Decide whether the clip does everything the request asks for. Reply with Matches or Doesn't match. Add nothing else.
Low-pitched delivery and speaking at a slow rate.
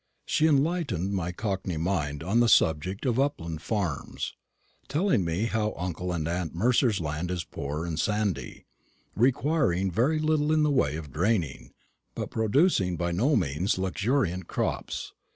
Doesn't match